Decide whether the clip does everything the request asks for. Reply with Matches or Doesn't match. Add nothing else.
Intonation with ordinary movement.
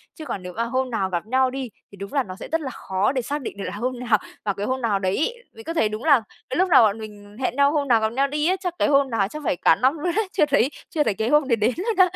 Doesn't match